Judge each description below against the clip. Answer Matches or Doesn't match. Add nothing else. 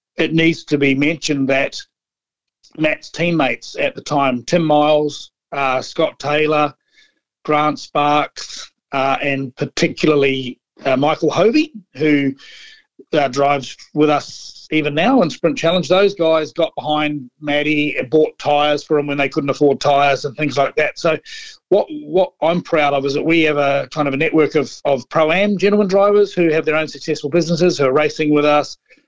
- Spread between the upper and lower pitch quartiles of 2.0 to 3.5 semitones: Matches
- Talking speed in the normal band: Matches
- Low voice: Doesn't match